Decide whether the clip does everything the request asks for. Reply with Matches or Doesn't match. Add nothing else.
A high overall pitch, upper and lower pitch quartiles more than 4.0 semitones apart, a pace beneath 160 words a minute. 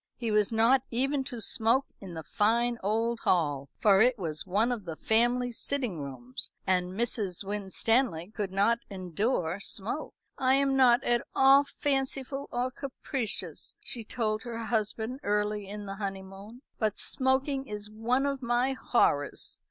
Matches